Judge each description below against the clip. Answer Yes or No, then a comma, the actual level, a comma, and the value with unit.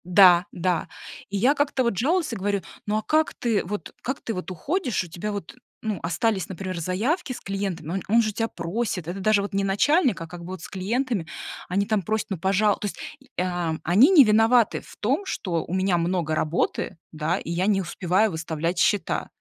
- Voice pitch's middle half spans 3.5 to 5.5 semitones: Yes, average, 4.3 semitones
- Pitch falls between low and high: No, high, 195 Hz